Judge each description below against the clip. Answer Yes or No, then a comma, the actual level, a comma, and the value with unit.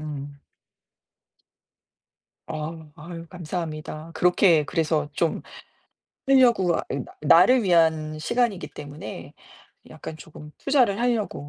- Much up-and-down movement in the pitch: No, average, 3.6 semitones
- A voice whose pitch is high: No, medium, 165 Hz